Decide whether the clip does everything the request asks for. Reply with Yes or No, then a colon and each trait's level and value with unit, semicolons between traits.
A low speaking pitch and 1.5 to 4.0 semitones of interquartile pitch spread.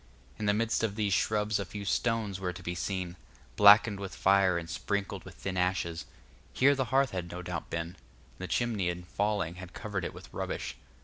Yes: very low, 95 Hz; average, 2.9 semitones